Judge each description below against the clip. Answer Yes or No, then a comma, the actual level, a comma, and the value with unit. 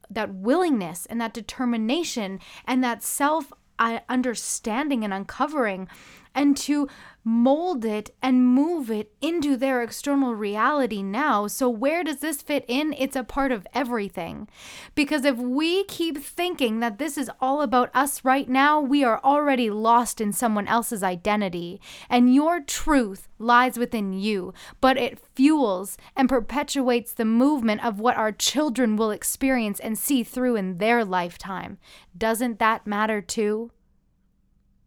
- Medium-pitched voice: No, high, 245 Hz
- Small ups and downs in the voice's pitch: No, average, 4.0 semitones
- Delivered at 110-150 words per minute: Yes, average, 145 wpm